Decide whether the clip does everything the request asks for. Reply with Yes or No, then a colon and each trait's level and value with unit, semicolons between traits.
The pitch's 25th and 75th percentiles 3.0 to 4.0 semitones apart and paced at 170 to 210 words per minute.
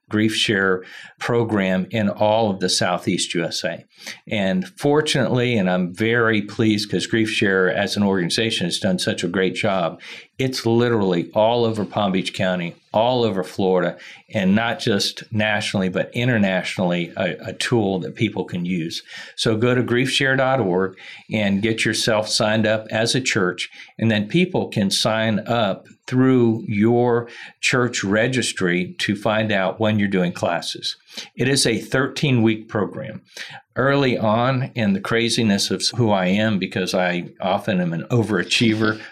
No: average, 3.6 semitones; average, 155 wpm